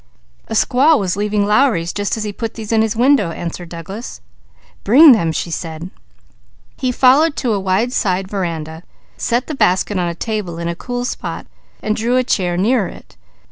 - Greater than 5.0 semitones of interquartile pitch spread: Yes, wide, 5.5 semitones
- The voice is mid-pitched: No, high, 210 Hz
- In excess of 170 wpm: Yes, average, 180 wpm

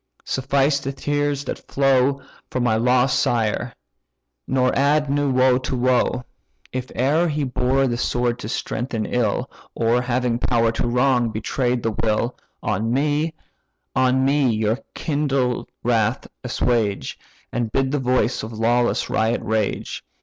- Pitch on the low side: Yes, low, 125 Hz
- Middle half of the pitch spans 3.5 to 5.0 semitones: No, narrow, 2.5 semitones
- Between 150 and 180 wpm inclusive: No, average, 140 wpm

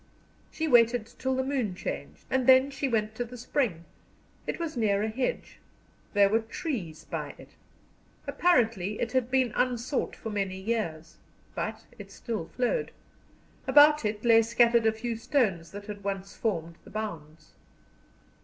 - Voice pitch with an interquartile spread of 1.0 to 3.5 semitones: No, average, 4.1 semitones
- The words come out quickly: No, average, 155 wpm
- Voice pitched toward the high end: Yes, high, 225 Hz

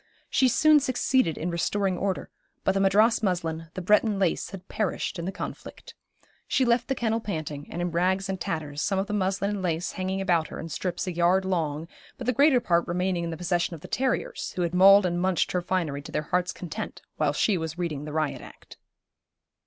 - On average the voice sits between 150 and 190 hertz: Yes, medium, 185 Hz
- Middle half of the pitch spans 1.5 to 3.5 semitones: Yes, average, 2.9 semitones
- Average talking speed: No, fast, 215 wpm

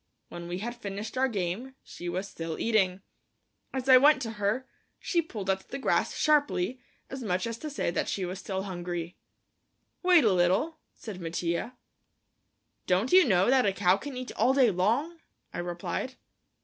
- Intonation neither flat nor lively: No, wide, 6.3 semitones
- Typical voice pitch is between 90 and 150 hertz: No, high, 205 Hz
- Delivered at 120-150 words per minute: No, average, 175 wpm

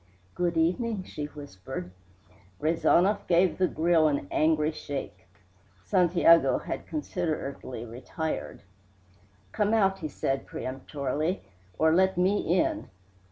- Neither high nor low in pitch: Yes, medium, 160 Hz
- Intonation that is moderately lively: Yes, average, 4.2 semitones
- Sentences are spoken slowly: Yes, slow, 110 wpm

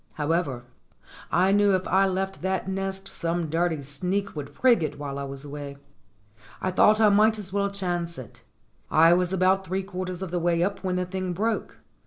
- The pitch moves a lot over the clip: No, average, 2.7 semitones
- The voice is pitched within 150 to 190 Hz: Yes, medium, 185 Hz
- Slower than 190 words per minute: No, average, 195 wpm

